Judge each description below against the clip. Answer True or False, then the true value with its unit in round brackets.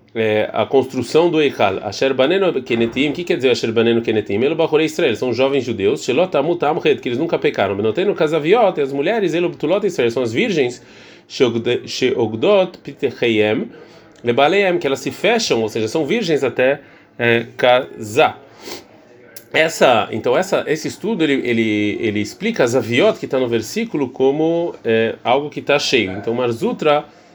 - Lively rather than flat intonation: True (6.0 semitones)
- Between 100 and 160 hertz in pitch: True (135 Hz)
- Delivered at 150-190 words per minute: False (120 wpm)